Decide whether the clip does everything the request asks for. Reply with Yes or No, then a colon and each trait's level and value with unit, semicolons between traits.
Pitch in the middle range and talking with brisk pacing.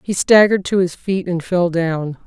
Yes: medium, 180 Hz; fast, 210 wpm